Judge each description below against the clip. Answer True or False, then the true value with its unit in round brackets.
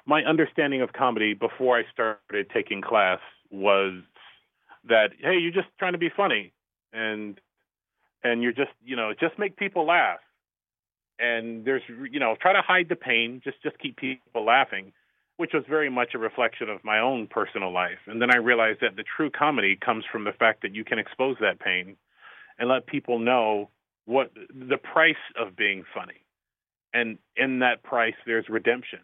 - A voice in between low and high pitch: False (125 Hz)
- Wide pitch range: True (5.7 semitones)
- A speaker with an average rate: True (180 wpm)